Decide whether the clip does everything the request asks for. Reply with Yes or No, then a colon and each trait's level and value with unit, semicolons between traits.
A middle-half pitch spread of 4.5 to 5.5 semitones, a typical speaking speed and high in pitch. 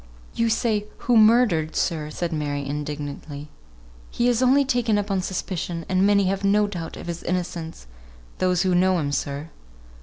No: average, 4.9 semitones; average, 170 wpm; medium, 180 Hz